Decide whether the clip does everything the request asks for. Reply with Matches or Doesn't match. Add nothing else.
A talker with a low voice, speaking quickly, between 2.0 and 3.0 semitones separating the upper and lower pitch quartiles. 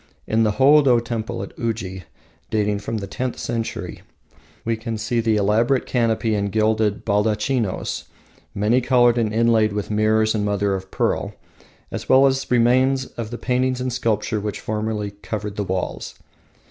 Doesn't match